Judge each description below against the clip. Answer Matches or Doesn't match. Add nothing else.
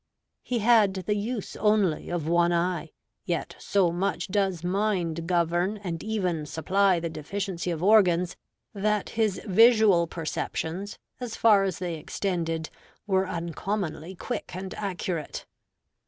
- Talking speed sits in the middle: Doesn't match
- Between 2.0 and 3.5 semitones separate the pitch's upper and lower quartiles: Matches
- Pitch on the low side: Doesn't match